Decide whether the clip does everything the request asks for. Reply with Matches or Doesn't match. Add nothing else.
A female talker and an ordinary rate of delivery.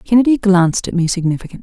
Matches